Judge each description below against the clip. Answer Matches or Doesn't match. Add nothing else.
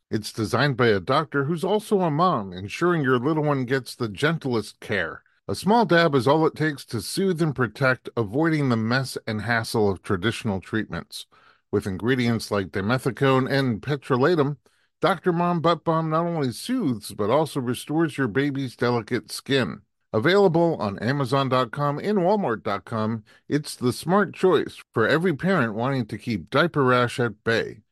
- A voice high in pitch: Doesn't match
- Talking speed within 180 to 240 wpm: Doesn't match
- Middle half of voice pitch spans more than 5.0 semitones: Matches